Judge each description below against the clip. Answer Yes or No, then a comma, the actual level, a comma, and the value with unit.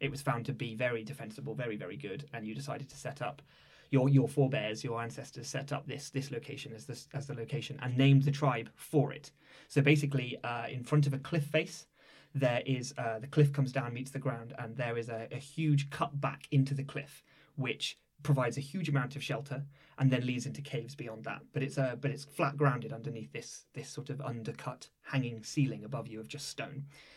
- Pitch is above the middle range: No, medium, 140 Hz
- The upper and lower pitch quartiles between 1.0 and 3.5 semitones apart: Yes, narrow, 2.4 semitones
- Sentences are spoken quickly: Yes, fast, 225 wpm